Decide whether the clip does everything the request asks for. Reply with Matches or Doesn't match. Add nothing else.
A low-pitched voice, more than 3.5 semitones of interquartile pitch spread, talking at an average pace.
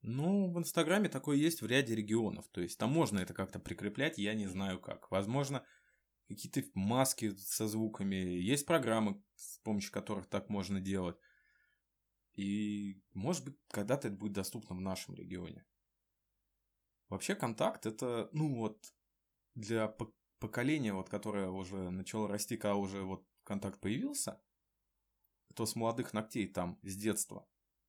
Doesn't match